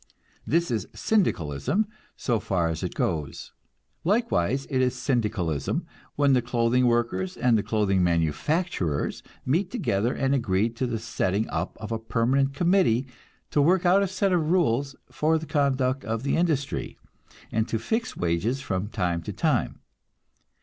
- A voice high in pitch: No, low, 125 Hz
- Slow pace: No, average, 155 wpm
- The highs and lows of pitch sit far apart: Yes, wide, 6.7 semitones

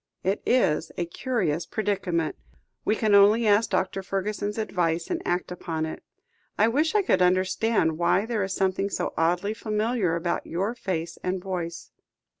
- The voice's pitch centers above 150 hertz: Yes, high, 190 Hz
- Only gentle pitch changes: No, average, 3.8 semitones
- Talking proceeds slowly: No, average, 160 wpm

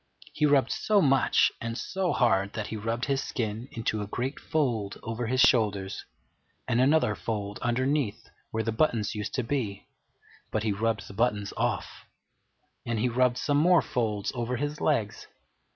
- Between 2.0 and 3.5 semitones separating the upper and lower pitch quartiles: No, average, 3.9 semitones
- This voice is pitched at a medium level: No, low, 115 Hz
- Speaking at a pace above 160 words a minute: Yes, average, 170 wpm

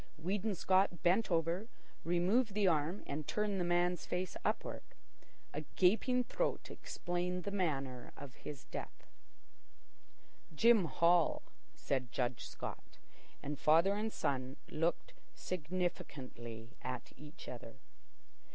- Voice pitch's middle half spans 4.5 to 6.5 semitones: Yes, average, 5.0 semitones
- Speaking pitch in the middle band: Yes, medium, 175 Hz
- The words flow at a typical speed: No, slow, 115 wpm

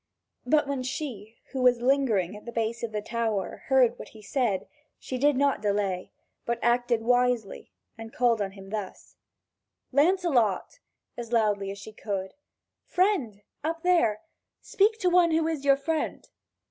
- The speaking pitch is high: Yes, high, 240 Hz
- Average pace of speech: Yes, average, 155 wpm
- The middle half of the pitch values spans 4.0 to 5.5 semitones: Yes, average, 5.0 semitones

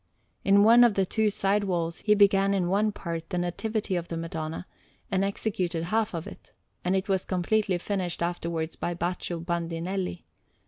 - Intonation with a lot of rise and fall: No, average, 2.8 semitones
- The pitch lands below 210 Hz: Yes, medium, 185 Hz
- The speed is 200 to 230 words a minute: No, average, 175 wpm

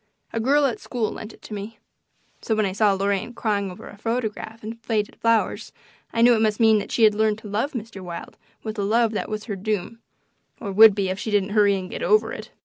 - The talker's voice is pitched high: Yes, high, 215 Hz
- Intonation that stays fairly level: Yes, narrow, 2.1 semitones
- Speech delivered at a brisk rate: Yes, fast, 240 wpm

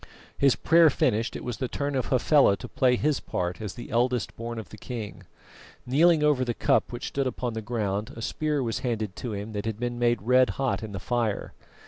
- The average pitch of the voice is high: No, low, 120 Hz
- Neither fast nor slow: No, fast, 220 wpm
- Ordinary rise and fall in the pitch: Yes, average, 3.0 semitones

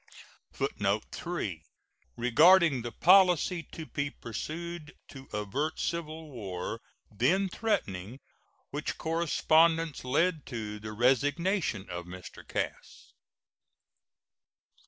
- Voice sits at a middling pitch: Yes, medium, 145 Hz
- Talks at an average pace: No, slow, 95 wpm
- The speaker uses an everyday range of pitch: No, wide, 7.6 semitones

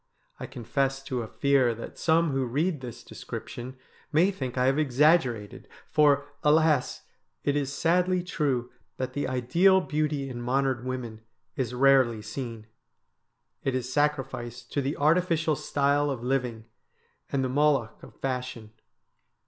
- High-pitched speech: No, low, 135 Hz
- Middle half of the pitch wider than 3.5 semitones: No, average, 3.2 semitones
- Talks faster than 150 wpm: No, average, 140 wpm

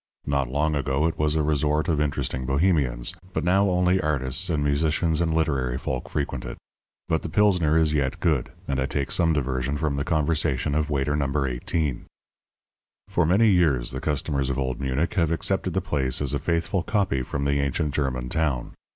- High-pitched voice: No, very low, 75 Hz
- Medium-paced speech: Yes, average, 190 wpm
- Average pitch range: Yes, average, 3.3 semitones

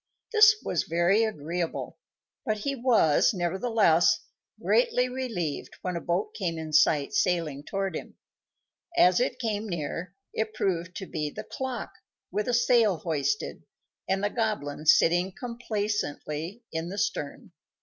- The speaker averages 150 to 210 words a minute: No, average, 140 wpm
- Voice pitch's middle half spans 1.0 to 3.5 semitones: No, average, 5.0 semitones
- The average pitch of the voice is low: No, high, 190 Hz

